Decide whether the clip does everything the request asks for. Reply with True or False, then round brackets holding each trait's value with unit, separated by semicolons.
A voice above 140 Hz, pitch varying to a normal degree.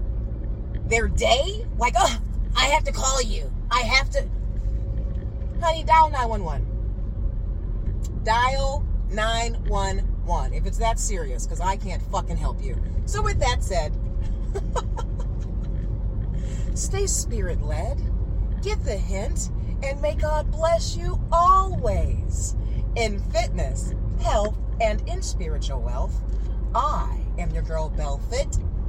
False (95 Hz; 3.4 semitones)